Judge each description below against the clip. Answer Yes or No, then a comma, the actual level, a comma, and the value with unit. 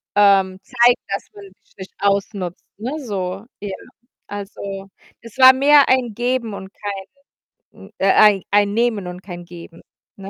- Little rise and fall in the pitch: No, average, 3.6 semitones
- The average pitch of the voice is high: Yes, high, 200 Hz